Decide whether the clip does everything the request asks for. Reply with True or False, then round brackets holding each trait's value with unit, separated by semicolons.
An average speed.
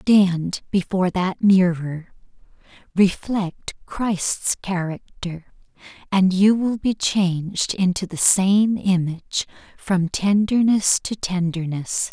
False (100 wpm)